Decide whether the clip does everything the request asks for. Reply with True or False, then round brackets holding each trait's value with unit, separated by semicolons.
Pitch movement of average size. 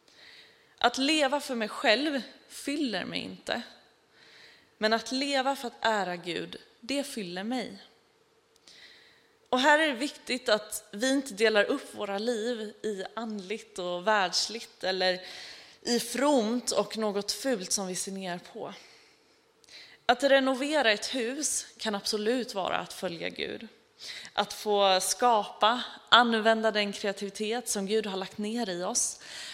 True (4.6 semitones)